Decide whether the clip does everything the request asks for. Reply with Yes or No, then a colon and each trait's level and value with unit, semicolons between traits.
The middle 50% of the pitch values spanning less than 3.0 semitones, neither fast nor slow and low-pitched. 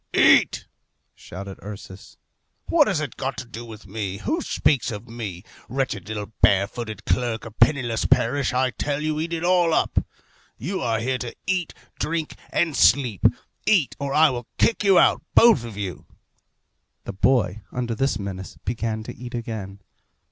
No: average, 5.3 semitones; average, 165 wpm; low, 120 Hz